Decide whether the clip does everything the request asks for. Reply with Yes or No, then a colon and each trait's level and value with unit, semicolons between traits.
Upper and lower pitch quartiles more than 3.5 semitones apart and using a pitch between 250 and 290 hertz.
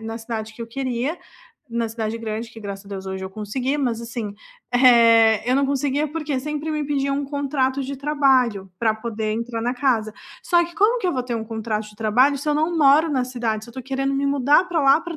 Yes: average, 4.1 semitones; very high, 255 Hz